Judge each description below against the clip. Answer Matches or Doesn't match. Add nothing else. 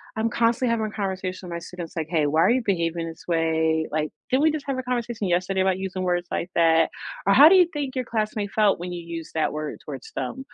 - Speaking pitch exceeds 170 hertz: Matches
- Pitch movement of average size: Doesn't match